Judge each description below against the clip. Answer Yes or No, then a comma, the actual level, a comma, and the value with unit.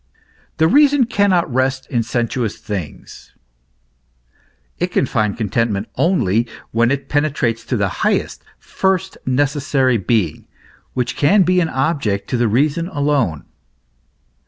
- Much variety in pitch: Yes, wide, 5.7 semitones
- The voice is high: No, low, 130 Hz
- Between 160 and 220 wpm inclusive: No, slow, 135 wpm